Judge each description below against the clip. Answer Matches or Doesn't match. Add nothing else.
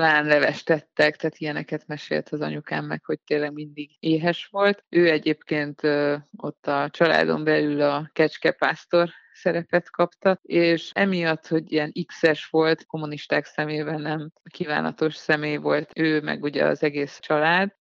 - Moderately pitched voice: Matches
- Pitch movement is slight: Matches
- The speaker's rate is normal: Matches